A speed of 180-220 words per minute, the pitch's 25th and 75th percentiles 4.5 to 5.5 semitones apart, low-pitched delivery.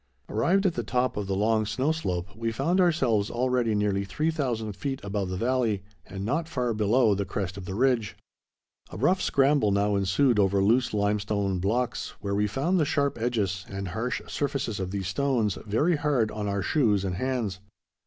Yes: average, 185 wpm; average, 4.8 semitones; low, 110 Hz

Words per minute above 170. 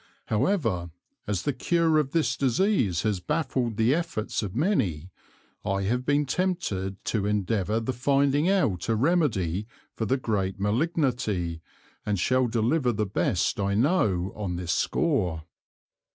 No: average, 140 wpm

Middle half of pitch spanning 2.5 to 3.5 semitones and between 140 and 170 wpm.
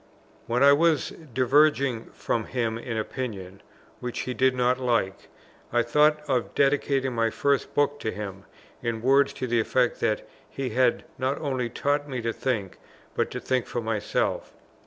Yes: average, 3.2 semitones; average, 165 wpm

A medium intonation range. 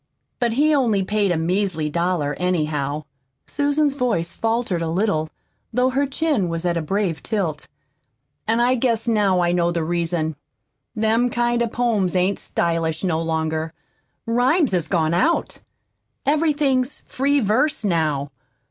No: wide, 6.7 semitones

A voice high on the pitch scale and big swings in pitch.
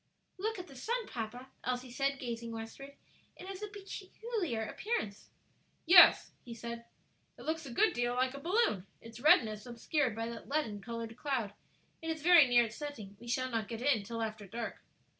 Yes: very high, 250 Hz; wide, 5.7 semitones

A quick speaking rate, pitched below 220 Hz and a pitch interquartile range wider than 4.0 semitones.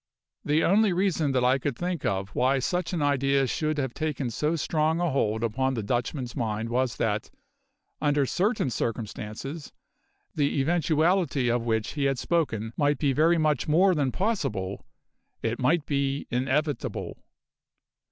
No: average, 150 wpm; medium, 140 Hz; average, 4.5 semitones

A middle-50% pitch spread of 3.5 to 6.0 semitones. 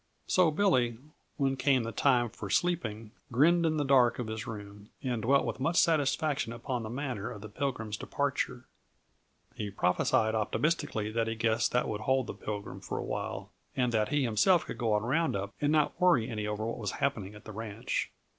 Yes: average, 4.4 semitones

